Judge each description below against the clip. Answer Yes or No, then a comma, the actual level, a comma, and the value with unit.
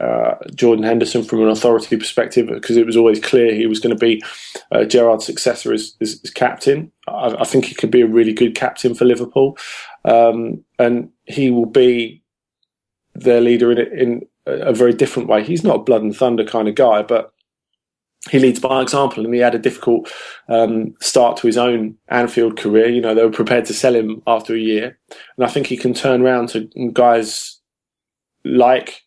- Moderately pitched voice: No, low, 120 Hz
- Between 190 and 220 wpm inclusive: Yes, average, 200 wpm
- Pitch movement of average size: No, narrow, 1.5 semitones